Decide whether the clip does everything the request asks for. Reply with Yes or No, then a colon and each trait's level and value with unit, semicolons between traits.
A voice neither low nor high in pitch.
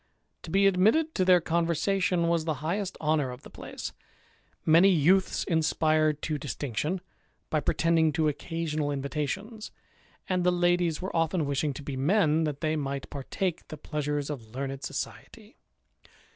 Yes: medium, 160 Hz